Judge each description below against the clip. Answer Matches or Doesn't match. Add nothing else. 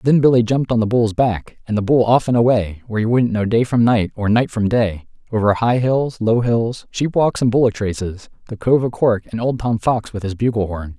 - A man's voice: Matches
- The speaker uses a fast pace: Matches